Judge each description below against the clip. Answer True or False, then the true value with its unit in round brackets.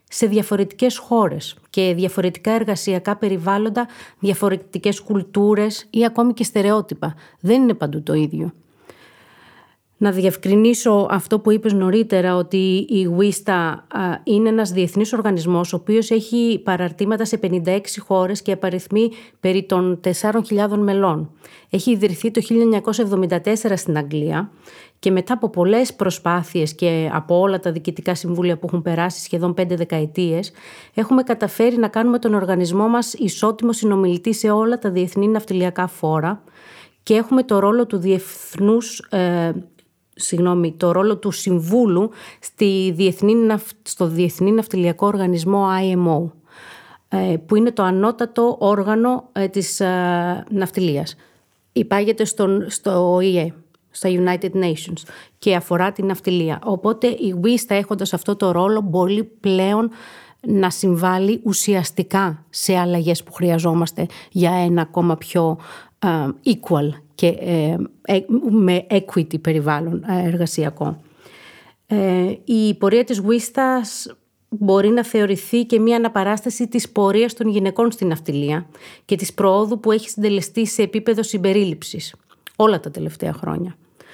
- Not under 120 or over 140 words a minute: True (130 wpm)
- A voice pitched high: True (195 Hz)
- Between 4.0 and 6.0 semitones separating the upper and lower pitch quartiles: False (3.4 semitones)